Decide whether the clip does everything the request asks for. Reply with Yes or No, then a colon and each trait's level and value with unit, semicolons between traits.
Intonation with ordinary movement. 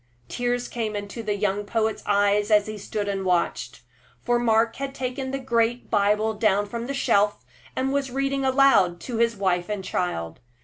Yes: average, 3.3 semitones